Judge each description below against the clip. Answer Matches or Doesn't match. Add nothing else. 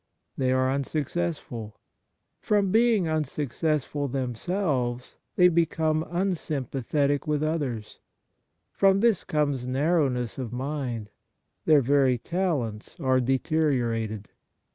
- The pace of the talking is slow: Matches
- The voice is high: Doesn't match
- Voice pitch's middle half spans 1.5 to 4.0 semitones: Doesn't match